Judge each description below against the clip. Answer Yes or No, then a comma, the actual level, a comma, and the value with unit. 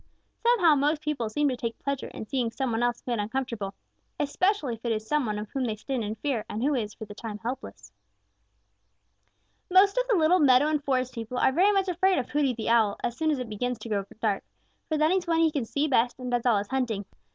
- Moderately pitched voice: No, very high, 255 Hz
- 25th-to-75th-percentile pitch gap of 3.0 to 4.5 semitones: No, average, 4.9 semitones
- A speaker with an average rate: No, fast, 245 wpm